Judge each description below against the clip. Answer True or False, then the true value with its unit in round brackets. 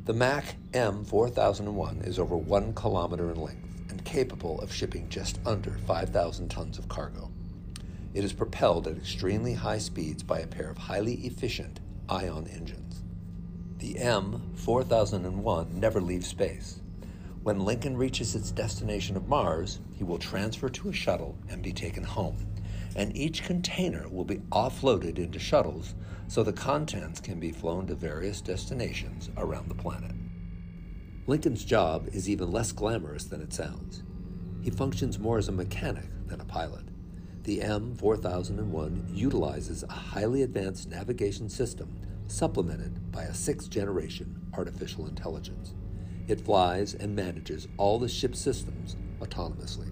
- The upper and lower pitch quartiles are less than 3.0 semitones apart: True (2.5 semitones)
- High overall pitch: False (95 Hz)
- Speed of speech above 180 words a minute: False (145 wpm)